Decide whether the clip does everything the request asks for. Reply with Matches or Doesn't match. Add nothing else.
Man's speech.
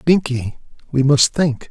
Matches